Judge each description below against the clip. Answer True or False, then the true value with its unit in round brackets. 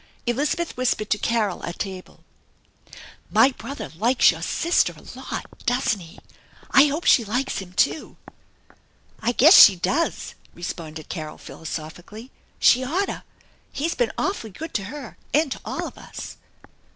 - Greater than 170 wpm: False (155 wpm)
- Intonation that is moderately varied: False (6.8 semitones)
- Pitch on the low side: False (235 Hz)